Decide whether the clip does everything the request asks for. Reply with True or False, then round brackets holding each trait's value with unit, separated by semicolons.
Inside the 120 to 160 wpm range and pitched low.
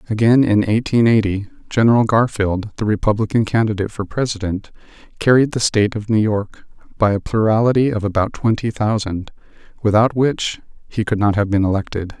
True (155 wpm; 110 Hz)